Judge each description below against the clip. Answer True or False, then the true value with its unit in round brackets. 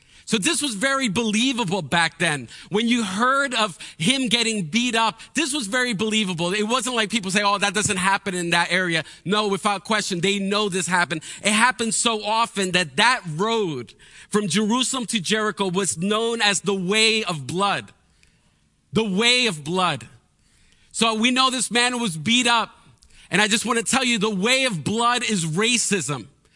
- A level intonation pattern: False (3.8 semitones)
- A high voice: True (210 Hz)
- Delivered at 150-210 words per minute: True (185 wpm)